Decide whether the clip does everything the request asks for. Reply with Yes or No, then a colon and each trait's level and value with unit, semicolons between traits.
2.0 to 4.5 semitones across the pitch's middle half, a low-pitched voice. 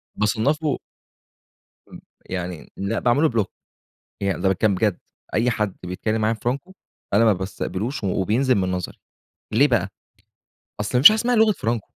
No: average, 4.9 semitones; low, 110 Hz